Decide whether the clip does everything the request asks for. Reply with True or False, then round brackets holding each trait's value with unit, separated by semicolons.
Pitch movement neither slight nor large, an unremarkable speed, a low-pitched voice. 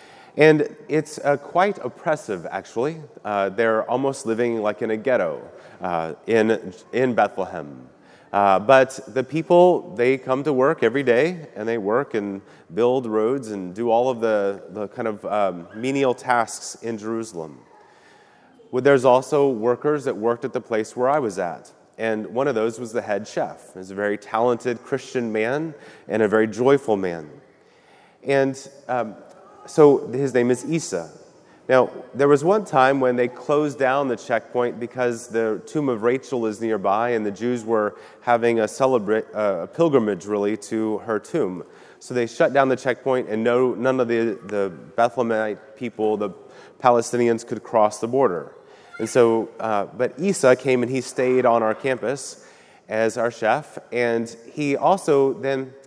True (3.5 semitones; 170 wpm; 120 Hz)